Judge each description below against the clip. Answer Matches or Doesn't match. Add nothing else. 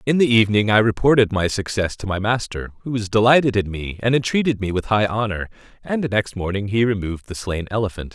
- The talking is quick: Matches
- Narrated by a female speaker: Doesn't match